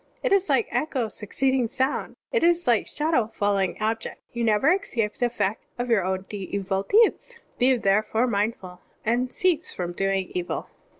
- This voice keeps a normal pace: Yes, average, 165 wpm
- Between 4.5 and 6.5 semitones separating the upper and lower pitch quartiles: Yes, average, 5.1 semitones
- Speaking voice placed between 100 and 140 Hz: No, high, 230 Hz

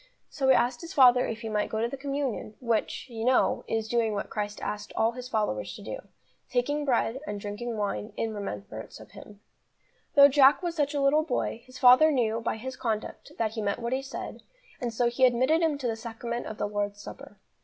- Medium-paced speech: No, fast, 220 wpm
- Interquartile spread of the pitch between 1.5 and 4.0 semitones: Yes, average, 3.7 semitones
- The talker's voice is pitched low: No, high, 235 Hz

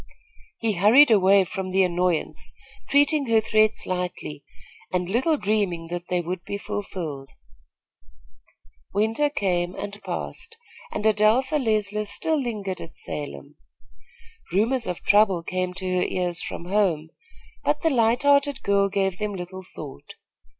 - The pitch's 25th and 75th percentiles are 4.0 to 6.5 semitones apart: No, average, 3.5 semitones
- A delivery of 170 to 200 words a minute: No, slow, 135 wpm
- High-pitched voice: Yes, high, 200 Hz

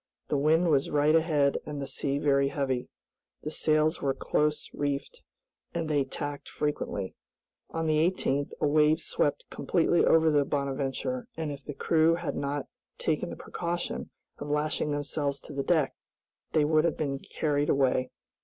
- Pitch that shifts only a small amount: Yes, narrow, 2.1 semitones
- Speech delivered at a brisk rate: No, average, 165 wpm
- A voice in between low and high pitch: Yes, medium, 150 Hz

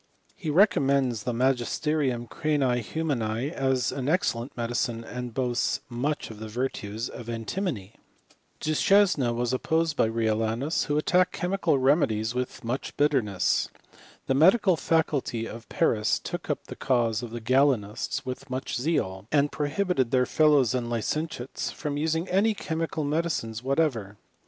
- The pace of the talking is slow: No, average, 150 wpm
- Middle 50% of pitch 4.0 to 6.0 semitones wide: Yes, average, 4.8 semitones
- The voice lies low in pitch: Yes, low, 130 Hz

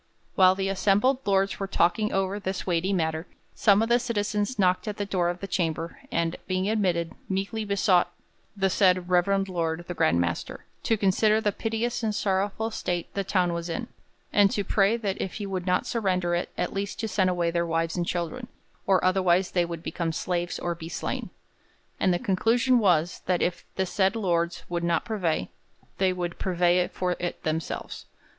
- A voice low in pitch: No, medium, 185 Hz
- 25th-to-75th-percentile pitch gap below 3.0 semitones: Yes, narrow, 2.6 semitones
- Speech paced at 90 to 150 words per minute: No, average, 190 wpm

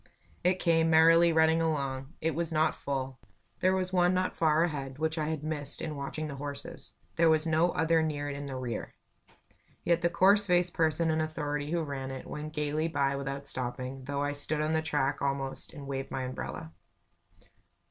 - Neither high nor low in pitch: Yes, medium, 155 Hz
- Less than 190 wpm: No, average, 195 wpm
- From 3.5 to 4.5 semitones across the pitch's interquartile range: No, average, 2.7 semitones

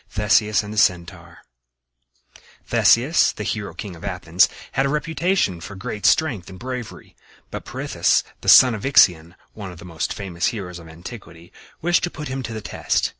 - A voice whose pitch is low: Yes, low, 105 Hz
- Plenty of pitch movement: Yes, wide, 6.4 semitones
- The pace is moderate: Yes, average, 175 wpm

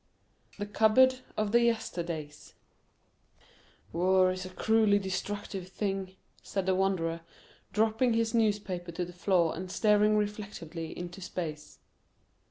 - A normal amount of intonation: Yes, average, 3.1 semitones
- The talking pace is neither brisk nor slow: No, slow, 120 wpm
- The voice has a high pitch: Yes, high, 195 Hz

